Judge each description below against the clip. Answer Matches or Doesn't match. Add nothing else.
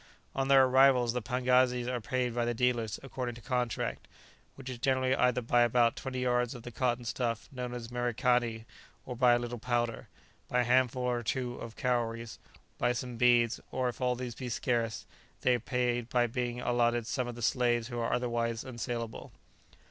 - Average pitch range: Doesn't match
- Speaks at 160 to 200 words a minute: Matches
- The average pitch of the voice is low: Matches